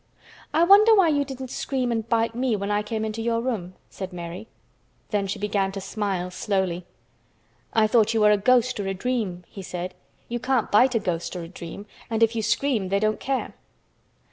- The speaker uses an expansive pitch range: No, average, 4.0 semitones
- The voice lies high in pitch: Yes, high, 215 Hz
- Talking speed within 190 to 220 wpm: Yes, fast, 205 wpm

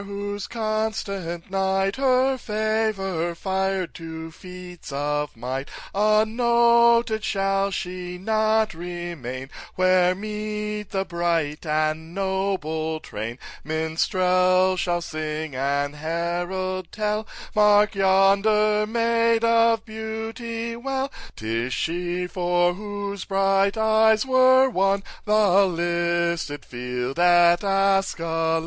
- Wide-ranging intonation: No, average, 3.9 semitones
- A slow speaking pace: Yes, slow, 100 wpm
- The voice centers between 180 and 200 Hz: Yes, high, 190 Hz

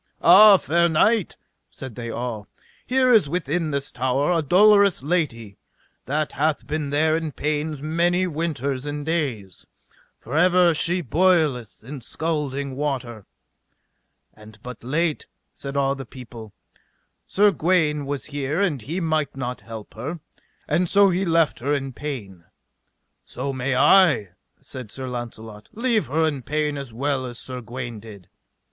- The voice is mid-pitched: Yes, medium, 145 Hz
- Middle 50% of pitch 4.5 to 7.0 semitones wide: Yes, average, 4.8 semitones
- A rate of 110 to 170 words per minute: Yes, average, 150 wpm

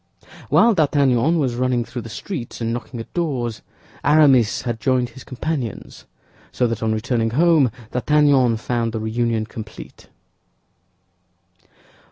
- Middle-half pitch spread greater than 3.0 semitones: Yes, average, 3.6 semitones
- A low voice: Yes, low, 120 Hz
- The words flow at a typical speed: No, slow, 130 wpm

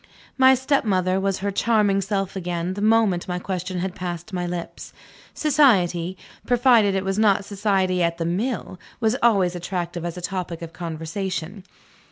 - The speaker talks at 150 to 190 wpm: Yes, average, 160 wpm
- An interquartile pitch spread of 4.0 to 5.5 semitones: No, average, 2.9 semitones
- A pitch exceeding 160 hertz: Yes, high, 190 Hz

